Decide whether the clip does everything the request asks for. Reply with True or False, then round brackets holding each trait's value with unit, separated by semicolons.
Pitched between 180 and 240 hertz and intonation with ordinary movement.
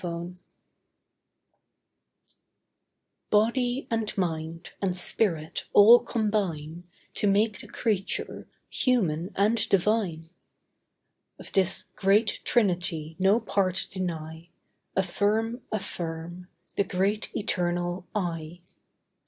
True (190 Hz; 3.7 semitones)